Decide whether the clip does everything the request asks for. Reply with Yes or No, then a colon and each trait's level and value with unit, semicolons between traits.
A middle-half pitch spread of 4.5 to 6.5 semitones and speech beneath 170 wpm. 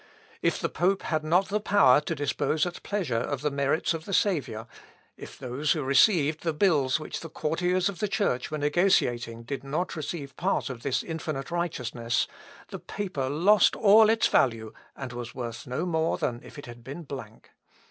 No: wide, 5.4 semitones; average, 190 wpm